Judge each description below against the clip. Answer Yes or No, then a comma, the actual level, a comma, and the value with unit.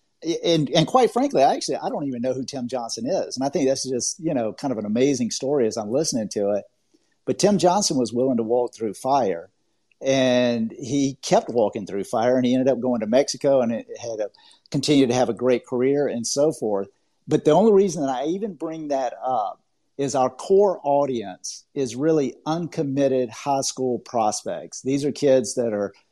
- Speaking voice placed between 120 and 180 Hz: Yes, low, 135 Hz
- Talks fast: Yes, fast, 210 wpm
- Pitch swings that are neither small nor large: Yes, average, 3.5 semitones